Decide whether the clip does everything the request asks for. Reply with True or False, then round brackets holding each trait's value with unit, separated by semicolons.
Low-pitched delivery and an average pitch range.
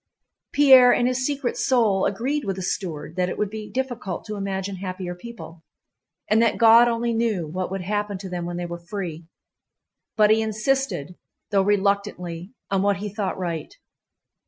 False (200 Hz; 4.1 semitones)